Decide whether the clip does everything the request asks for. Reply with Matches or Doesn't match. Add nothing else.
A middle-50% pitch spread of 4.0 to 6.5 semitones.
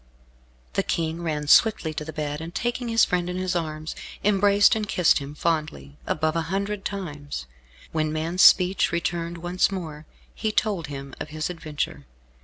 Doesn't match